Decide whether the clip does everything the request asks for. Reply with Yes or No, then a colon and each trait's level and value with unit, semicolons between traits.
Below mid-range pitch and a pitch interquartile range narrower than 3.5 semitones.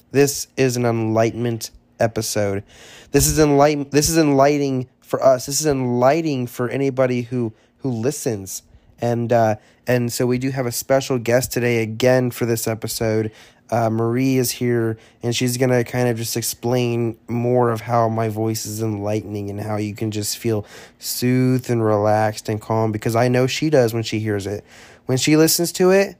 Yes: low, 120 Hz; narrow, 2.5 semitones